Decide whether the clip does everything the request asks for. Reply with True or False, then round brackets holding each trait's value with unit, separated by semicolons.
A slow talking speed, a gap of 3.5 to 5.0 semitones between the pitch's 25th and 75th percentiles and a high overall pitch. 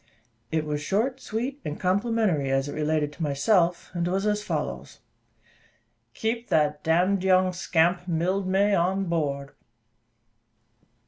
False (130 wpm; 4.6 semitones; 180 Hz)